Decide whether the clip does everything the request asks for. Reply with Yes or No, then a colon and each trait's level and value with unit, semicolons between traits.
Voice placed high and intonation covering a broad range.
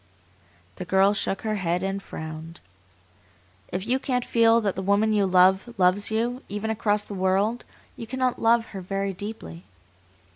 No: high, 200 Hz; average, 3.2 semitones